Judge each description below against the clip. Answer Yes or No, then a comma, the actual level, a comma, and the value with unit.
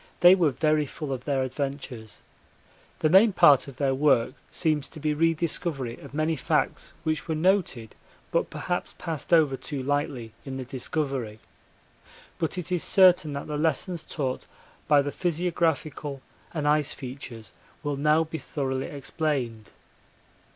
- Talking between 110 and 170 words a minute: Yes, average, 150 wpm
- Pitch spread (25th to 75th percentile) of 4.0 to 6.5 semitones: No, average, 3.3 semitones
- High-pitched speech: No, medium, 150 Hz